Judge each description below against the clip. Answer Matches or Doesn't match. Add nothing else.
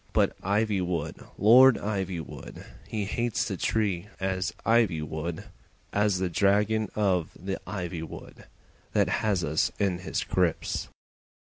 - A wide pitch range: Doesn't match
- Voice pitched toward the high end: Doesn't match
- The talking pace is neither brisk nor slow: Doesn't match